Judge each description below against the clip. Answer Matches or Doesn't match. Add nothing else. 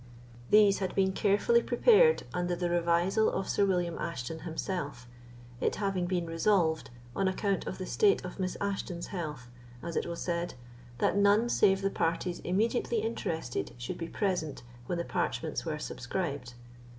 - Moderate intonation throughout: Matches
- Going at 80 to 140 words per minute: Doesn't match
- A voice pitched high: Doesn't match